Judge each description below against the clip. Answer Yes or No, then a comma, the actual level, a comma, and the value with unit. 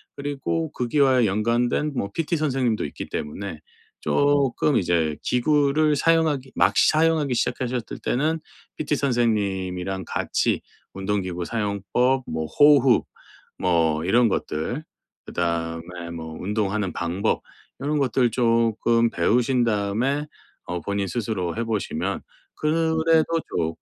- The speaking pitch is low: Yes, low, 115 Hz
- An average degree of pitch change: No, wide, 6.9 semitones